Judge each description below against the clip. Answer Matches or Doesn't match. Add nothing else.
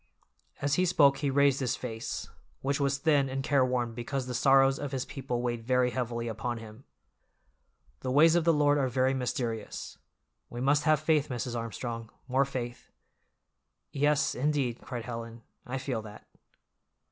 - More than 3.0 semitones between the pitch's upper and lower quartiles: Doesn't match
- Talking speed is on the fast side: Doesn't match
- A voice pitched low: Matches